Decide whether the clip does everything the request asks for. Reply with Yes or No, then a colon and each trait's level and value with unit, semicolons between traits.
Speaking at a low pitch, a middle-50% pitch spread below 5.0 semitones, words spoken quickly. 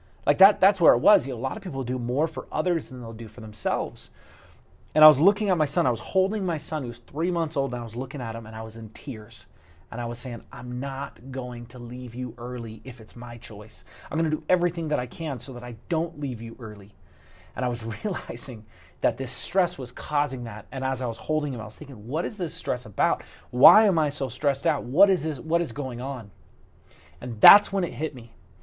No: low, 125 Hz; average, 5.3 semitones; fast, 255 wpm